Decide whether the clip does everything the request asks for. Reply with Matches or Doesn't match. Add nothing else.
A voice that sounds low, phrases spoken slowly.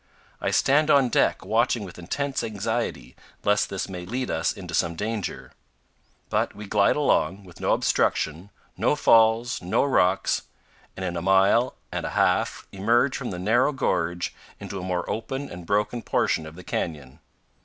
Doesn't match